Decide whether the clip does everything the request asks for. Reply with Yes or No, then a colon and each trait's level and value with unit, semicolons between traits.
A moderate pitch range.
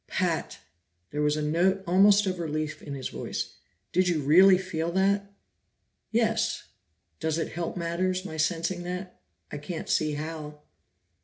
Yes: average, 3.3 semitones